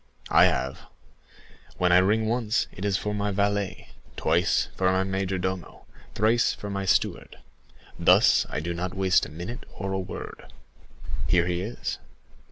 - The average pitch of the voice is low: Yes, very low, 95 Hz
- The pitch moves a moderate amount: No, narrow, 2.2 semitones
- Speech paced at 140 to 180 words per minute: Yes, average, 150 wpm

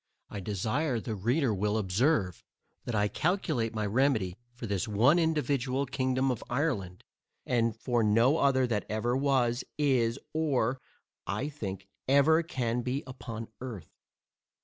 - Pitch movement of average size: Yes, average, 4.2 semitones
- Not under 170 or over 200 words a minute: No, average, 140 wpm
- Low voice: Yes, low, 120 Hz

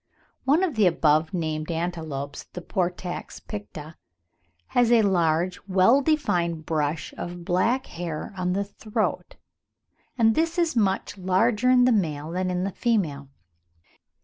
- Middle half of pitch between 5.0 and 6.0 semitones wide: Yes, wide, 5.5 semitones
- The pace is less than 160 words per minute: Yes, average, 140 wpm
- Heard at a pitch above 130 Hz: Yes, medium, 185 Hz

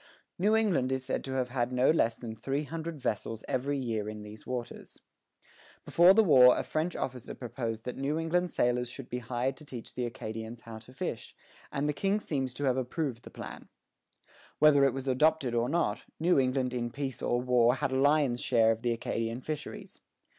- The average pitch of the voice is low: Yes, low, 130 Hz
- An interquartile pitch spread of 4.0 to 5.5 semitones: No, average, 3.4 semitones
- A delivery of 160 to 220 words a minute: Yes, average, 200 wpm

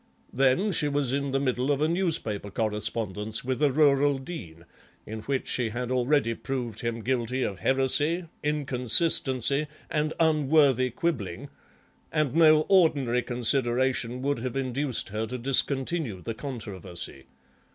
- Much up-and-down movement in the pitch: No, average, 4.0 semitones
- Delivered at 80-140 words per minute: Yes, slow, 135 wpm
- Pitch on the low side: Yes, low, 130 Hz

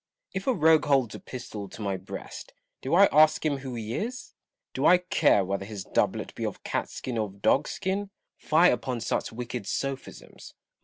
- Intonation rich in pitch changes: Yes, wide, 6.7 semitones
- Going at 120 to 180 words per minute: No, average, 195 wpm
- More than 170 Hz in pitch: No, low, 130 Hz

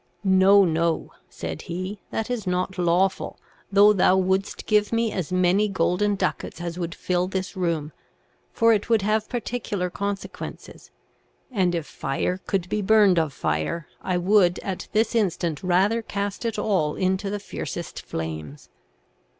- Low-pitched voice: No, high, 190 Hz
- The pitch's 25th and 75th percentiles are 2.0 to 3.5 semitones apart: Yes, average, 2.9 semitones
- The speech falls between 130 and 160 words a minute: Yes, average, 150 wpm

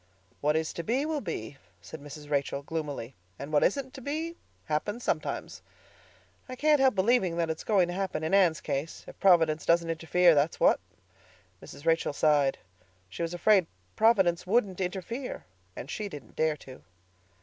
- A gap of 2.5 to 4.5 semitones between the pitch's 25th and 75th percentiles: No, wide, 5.4 semitones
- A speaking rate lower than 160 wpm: No, average, 165 wpm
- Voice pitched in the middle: Yes, medium, 170 Hz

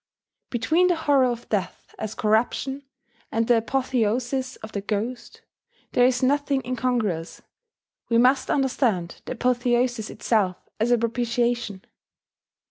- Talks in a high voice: Yes, high, 240 Hz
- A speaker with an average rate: No, slow, 125 wpm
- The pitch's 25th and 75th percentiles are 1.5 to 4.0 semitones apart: Yes, average, 2.7 semitones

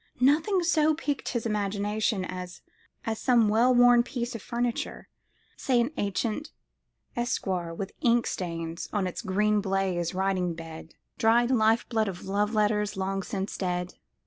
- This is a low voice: No, high, 210 Hz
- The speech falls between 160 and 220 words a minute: No, average, 140 wpm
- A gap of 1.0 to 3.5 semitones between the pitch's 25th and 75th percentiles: No, average, 4.0 semitones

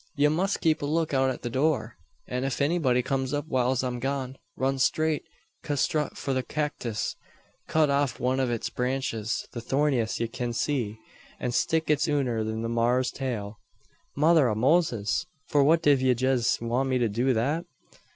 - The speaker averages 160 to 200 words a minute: Yes, average, 175 wpm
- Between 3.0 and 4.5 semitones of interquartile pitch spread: Yes, average, 3.3 semitones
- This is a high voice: No, low, 130 Hz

